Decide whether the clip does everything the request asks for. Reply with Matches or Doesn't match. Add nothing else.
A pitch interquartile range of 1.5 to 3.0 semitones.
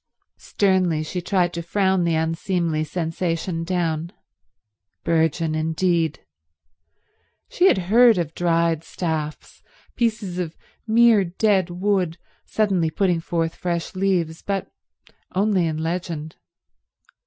Matches